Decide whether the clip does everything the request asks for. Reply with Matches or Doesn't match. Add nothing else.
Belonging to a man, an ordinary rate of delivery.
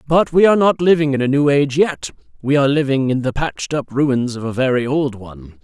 Doesn't match